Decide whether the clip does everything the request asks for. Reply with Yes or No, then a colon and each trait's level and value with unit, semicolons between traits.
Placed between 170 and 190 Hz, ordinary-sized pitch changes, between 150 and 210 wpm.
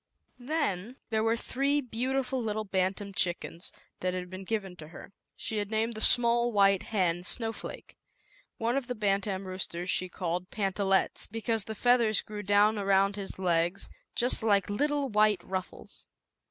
No: high, 205 Hz; average, 3.3 semitones; average, 155 wpm